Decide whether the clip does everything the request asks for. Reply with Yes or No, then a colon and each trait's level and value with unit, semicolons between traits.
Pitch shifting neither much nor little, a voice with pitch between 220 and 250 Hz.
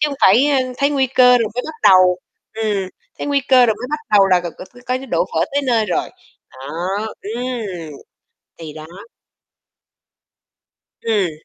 No: wide, 6.0 semitones; high, 225 Hz